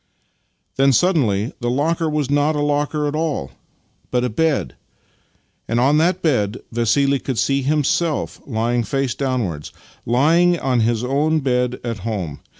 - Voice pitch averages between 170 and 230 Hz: No, low, 135 Hz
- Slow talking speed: No, average, 155 wpm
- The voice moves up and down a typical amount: Yes, average, 4.2 semitones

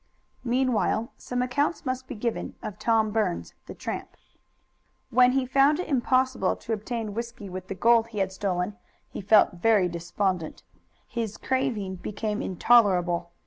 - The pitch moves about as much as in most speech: Yes, average, 4.5 semitones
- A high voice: Yes, high, 220 Hz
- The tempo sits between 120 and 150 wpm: Yes, average, 145 wpm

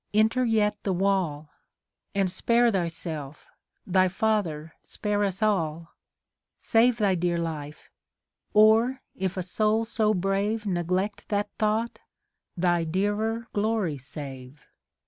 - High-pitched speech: Yes, high, 195 Hz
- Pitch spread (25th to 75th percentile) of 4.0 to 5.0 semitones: Yes, average, 4.3 semitones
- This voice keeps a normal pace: No, slow, 115 wpm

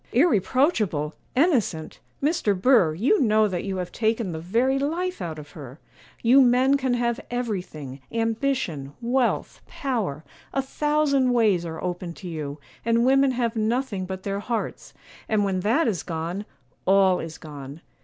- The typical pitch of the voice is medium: No, high, 215 Hz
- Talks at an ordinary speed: Yes, average, 155 wpm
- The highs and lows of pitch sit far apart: Yes, wide, 6.6 semitones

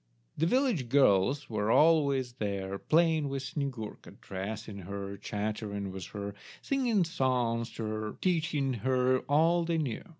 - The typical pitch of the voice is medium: No, low, 130 Hz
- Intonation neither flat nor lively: No, wide, 6.9 semitones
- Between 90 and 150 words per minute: Yes, slow, 135 wpm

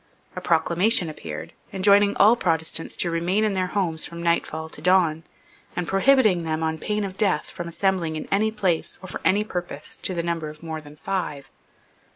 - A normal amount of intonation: Yes, average, 3.4 semitones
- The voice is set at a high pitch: No, medium, 175 Hz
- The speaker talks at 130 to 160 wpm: No, average, 190 wpm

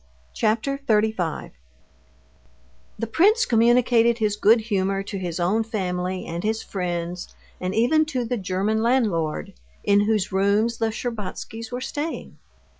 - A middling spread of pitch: Yes, average, 3.8 semitones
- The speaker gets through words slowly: Yes, slow, 130 wpm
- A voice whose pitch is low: No, high, 220 Hz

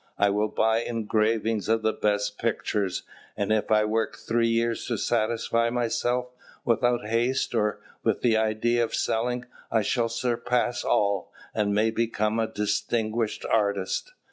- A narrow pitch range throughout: Yes, narrow, 1.6 semitones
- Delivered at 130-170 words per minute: Yes, average, 145 wpm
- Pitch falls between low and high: No, low, 110 Hz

